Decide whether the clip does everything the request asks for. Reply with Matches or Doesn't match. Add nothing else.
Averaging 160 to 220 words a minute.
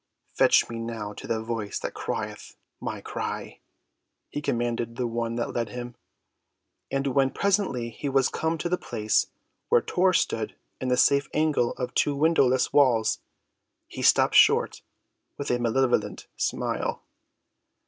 Doesn't match